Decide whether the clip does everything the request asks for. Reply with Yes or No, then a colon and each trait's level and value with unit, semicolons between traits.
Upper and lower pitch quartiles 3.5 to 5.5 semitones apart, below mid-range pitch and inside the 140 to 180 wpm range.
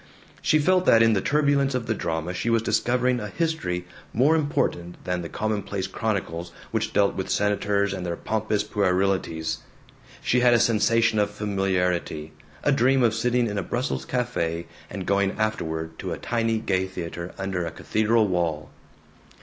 Yes: average, 4.5 semitones; low, 105 Hz; average, 165 wpm